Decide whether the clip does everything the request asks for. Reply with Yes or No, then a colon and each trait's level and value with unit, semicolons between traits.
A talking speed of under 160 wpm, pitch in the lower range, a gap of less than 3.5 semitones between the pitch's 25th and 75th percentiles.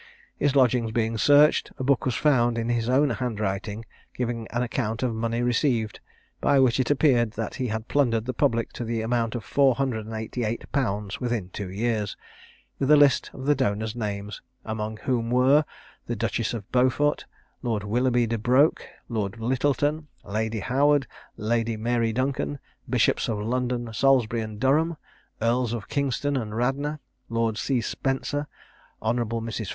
No: average, 165 wpm; low, 120 Hz; average, 2.9 semitones